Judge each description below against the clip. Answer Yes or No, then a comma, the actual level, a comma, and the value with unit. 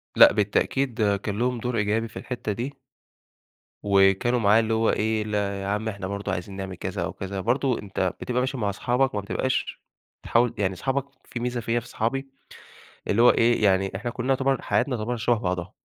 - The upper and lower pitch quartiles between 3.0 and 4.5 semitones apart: Yes, average, 3.5 semitones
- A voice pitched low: Yes, low, 110 Hz